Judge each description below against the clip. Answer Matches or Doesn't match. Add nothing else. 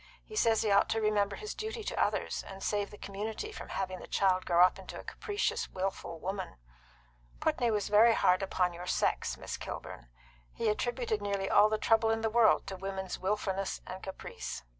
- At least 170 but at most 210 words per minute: Matches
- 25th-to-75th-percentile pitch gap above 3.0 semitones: Doesn't match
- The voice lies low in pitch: Doesn't match